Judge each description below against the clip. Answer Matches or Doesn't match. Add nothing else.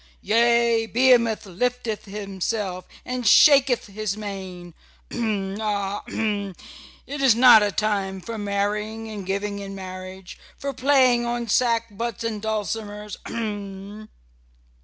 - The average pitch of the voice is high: Matches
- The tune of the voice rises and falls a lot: Doesn't match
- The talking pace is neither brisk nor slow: Doesn't match